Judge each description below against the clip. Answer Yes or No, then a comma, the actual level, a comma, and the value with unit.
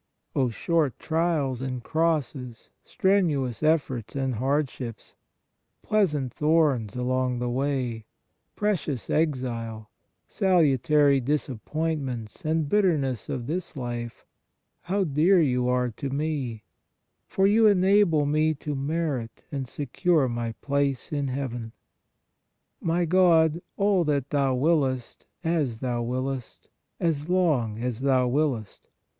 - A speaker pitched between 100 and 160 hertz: Yes, medium, 140 Hz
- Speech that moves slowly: Yes, slow, 115 wpm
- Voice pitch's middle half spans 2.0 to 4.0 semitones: No, average, 4.4 semitones